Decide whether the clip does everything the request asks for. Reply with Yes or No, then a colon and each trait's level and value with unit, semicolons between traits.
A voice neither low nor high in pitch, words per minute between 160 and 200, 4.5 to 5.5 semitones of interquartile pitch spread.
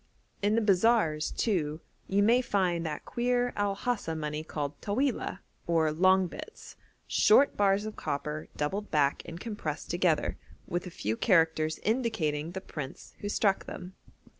No: medium, 180 Hz; average, 150 wpm; average, 5.1 semitones